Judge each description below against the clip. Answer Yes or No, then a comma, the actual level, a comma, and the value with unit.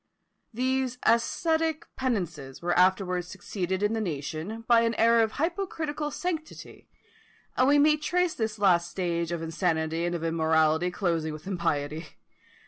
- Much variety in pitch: Yes, wide, 7.6 semitones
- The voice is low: No, high, 190 Hz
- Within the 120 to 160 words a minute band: Yes, average, 140 wpm